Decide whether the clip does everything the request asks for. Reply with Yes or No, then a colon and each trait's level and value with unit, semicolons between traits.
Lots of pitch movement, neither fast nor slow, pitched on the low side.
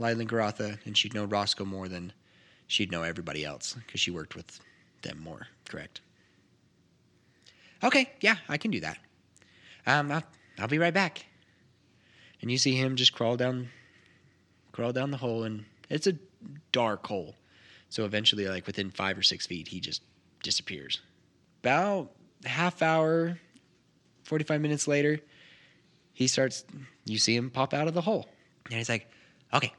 Yes: wide, 6.3 semitones; average, 160 wpm; low, 130 Hz